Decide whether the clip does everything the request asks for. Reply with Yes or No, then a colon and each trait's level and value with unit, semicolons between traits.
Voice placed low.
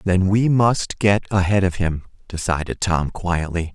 Yes: very low, 95 Hz